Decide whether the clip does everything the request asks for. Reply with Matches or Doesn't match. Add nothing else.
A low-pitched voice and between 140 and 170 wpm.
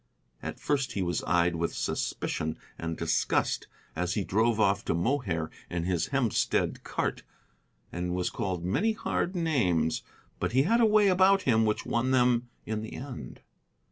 Matches